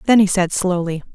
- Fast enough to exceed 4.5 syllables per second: Yes, 5.6 syllables/s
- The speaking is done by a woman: Yes, female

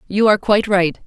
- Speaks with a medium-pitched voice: No, high, 200 Hz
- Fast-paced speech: Yes, fast, 225 wpm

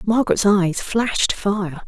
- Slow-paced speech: Yes, slow, 130 wpm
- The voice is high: Yes, high, 200 Hz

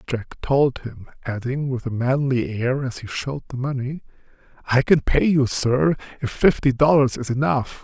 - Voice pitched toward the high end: No, low, 130 Hz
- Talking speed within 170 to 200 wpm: Yes, average, 175 wpm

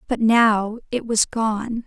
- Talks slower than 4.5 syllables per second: Yes, 3.2 syllables/s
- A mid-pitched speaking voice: No, high, 225 Hz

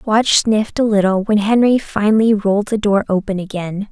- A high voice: Yes, high, 210 Hz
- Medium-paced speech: Yes, average, 185 wpm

